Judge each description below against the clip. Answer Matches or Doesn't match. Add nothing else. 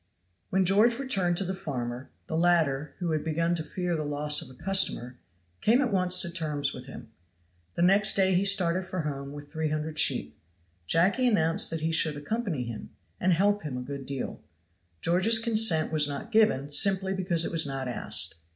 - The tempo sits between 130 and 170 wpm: Doesn't match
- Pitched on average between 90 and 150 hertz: Doesn't match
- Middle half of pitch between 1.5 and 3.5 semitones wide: Doesn't match